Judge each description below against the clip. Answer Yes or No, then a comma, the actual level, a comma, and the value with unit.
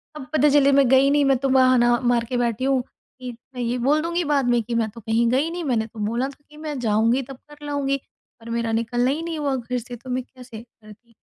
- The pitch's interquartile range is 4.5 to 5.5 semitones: No, average, 2.9 semitones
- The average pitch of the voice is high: Yes, very high, 255 Hz